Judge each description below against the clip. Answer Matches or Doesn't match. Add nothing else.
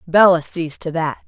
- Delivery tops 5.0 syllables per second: Doesn't match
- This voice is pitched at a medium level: Matches